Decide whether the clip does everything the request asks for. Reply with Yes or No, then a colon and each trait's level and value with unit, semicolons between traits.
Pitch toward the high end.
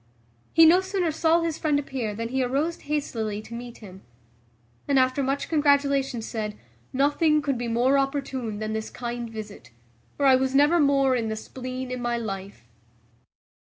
Yes: very high, 260 Hz